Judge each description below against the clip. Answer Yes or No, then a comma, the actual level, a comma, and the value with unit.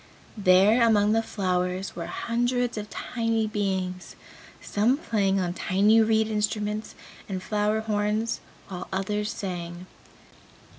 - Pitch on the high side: Yes, high, 210 Hz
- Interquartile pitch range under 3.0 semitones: Yes, narrow, 2.6 semitones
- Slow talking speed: Yes, slow, 115 wpm